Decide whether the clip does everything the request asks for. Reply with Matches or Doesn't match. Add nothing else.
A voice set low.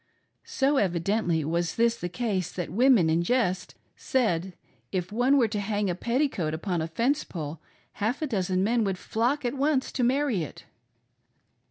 Doesn't match